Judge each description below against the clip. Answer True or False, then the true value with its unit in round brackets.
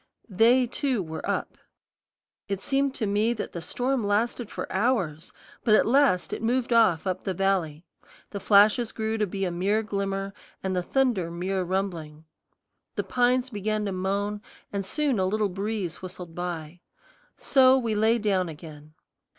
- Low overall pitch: False (200 Hz)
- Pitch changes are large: False (4.0 semitones)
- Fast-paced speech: False (165 wpm)